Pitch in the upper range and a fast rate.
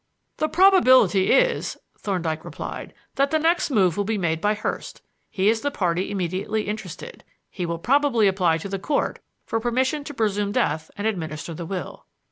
No: high, 205 Hz; average, 175 wpm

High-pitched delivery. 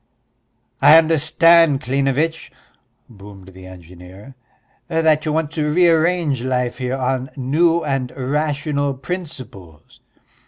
No: medium, 140 Hz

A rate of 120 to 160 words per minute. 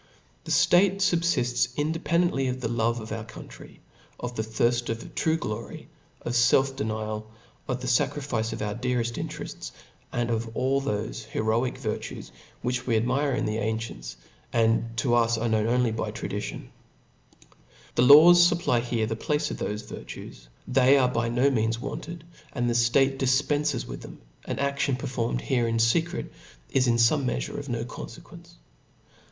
No: average, 170 wpm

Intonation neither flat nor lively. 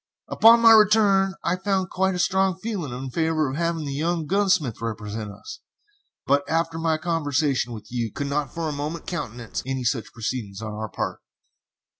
No: wide, 6.9 semitones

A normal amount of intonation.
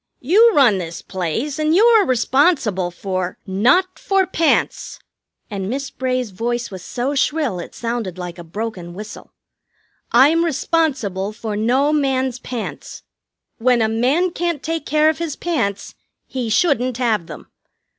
No: wide, 6.7 semitones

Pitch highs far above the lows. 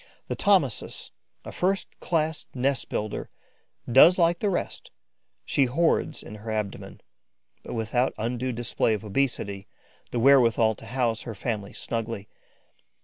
No: average, 4.1 semitones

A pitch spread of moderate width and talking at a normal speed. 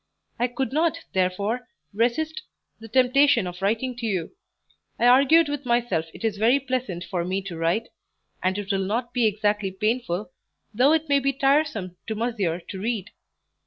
Yes: average, 5.0 semitones; average, 170 wpm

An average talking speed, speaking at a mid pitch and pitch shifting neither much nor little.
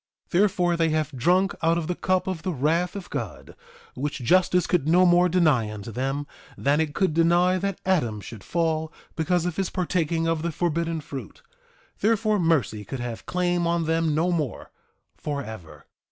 Yes: average, 180 wpm; medium, 165 Hz; average, 3.4 semitones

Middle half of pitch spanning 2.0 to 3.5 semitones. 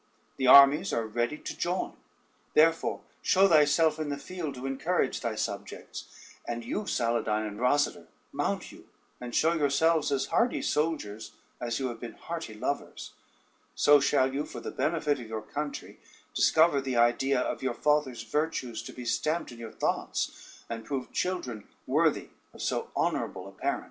No: average, 4.7 semitones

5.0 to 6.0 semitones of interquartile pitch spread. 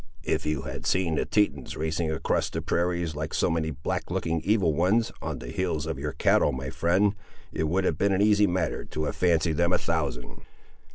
No: average, 3.3 semitones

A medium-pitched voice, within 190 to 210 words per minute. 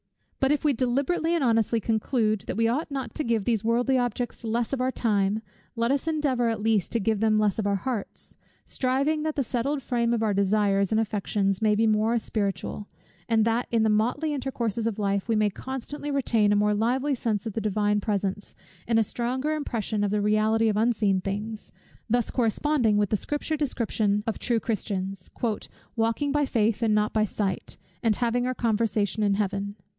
No: high, 225 Hz; average, 195 wpm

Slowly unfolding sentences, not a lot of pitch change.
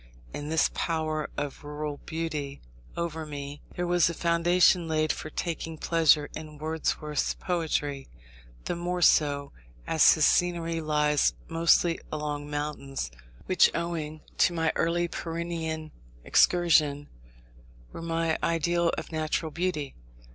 Yes: slow, 125 wpm; narrow, 2.1 semitones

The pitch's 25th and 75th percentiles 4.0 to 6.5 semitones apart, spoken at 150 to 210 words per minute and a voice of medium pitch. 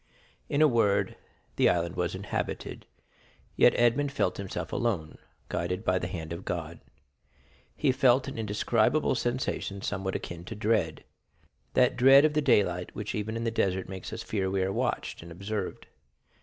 No: average, 4.5 semitones; average, 160 wpm; low, 100 Hz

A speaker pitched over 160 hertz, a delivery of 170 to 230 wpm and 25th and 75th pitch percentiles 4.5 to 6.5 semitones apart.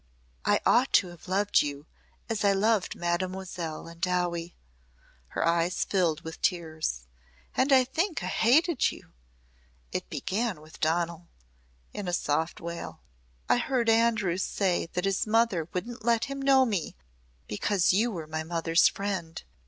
No: medium, 185 Hz; average, 150 wpm; average, 5.1 semitones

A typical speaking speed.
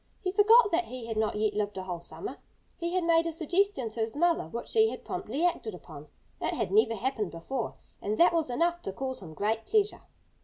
No: fast, 225 wpm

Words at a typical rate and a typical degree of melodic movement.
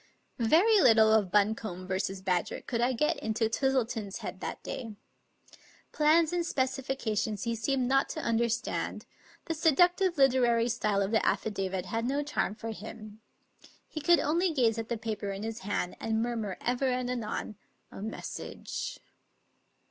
Yes: average, 165 wpm; average, 3.9 semitones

